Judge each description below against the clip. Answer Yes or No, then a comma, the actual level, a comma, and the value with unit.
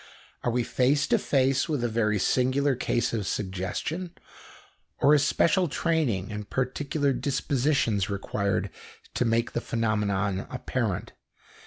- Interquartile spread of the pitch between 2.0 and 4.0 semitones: No, average, 5.1 semitones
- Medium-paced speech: No, slow, 130 wpm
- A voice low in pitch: Yes, low, 120 Hz